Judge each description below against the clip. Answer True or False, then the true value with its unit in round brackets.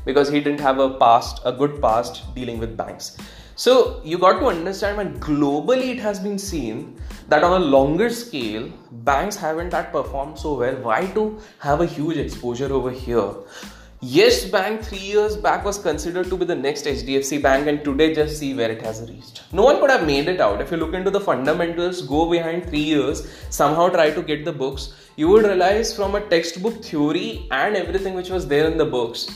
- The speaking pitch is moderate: True (165 Hz)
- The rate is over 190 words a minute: True (205 wpm)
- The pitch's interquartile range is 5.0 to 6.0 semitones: True (5.6 semitones)